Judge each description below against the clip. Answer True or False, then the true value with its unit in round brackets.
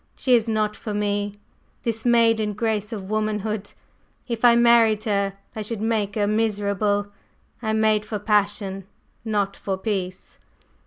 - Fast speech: False (150 wpm)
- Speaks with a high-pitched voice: True (215 Hz)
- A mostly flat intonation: True (1.6 semitones)